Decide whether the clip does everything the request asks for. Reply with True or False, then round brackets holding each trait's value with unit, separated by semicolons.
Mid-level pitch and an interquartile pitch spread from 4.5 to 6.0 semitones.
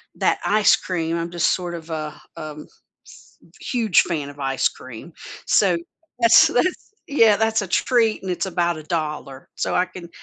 True (175 Hz; 5.1 semitones)